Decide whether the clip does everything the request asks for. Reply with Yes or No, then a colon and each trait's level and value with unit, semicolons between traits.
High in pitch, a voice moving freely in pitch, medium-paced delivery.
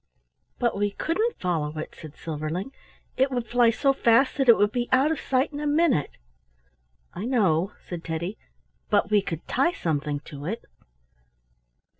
Yes: high, 215 Hz; wide, 8.2 semitones; average, 165 wpm